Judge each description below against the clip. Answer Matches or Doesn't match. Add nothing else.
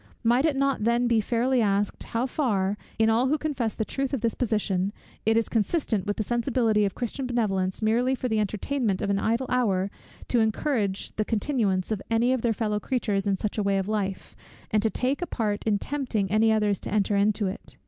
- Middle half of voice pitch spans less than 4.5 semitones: Matches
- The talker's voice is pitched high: Matches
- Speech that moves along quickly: Matches